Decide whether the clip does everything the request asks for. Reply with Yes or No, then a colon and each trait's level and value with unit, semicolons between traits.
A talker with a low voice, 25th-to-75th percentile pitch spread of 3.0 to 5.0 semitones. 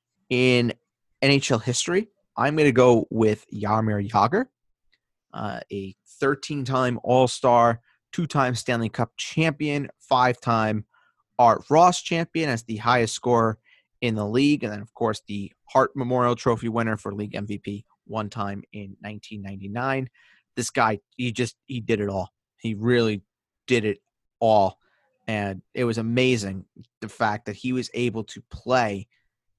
Yes: low, 115 Hz; average, 3.3 semitones